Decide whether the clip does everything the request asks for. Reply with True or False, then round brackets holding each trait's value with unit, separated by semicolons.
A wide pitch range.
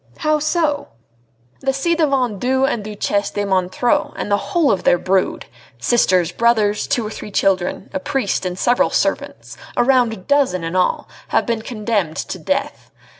True (5.8 semitones)